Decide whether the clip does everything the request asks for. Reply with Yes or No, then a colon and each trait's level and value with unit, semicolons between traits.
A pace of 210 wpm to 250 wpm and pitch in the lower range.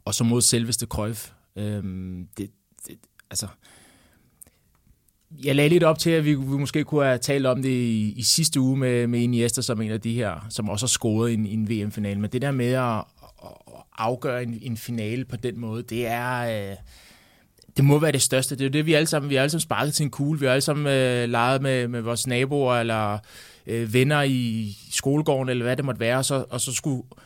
Yes: fast, 225 wpm; low, 125 Hz